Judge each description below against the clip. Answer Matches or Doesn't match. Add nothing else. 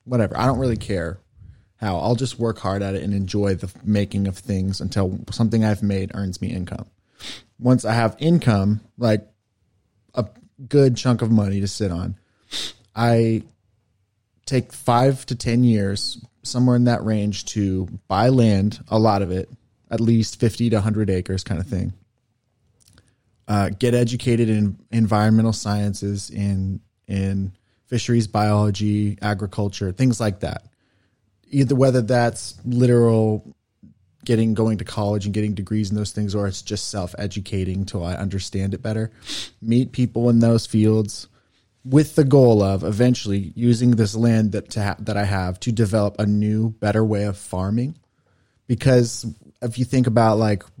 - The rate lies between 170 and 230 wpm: Doesn't match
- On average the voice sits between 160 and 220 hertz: Doesn't match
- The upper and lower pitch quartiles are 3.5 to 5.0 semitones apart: Doesn't match